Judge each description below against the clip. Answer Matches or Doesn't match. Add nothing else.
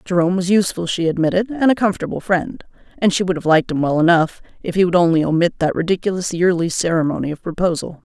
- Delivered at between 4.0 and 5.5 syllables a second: Doesn't match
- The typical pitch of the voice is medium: Matches